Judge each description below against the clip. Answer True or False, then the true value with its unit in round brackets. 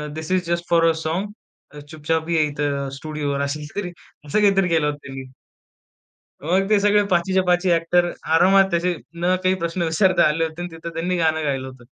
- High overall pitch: False (165 Hz)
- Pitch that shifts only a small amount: False (3.1 semitones)